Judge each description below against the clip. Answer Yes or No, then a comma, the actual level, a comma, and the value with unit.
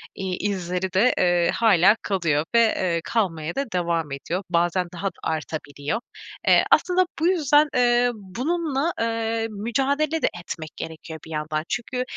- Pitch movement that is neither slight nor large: No, wide, 6.3 semitones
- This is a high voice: Yes, high, 195 Hz